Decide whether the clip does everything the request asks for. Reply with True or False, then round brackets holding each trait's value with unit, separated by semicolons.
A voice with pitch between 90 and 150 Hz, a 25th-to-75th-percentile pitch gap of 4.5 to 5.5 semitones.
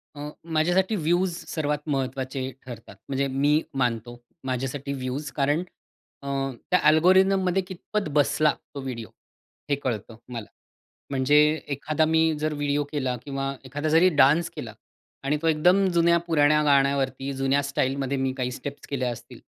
False (140 Hz; 3.0 semitones)